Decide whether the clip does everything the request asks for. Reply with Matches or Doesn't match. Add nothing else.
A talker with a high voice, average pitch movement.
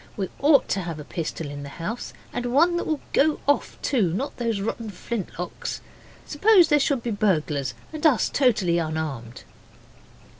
Doesn't match